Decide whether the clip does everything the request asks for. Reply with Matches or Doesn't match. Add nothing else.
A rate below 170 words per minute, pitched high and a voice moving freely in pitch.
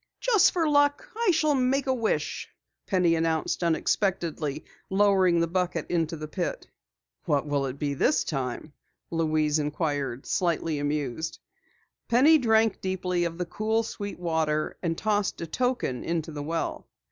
Doesn't match